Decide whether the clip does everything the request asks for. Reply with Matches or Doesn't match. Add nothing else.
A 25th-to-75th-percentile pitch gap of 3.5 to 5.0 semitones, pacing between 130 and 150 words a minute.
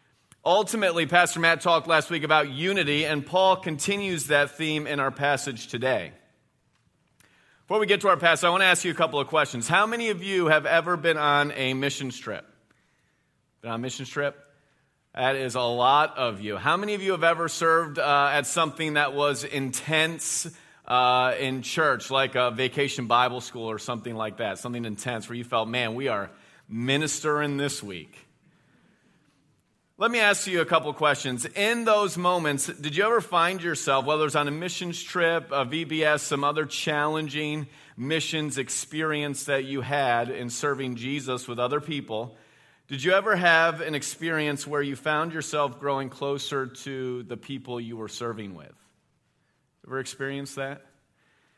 Doesn't match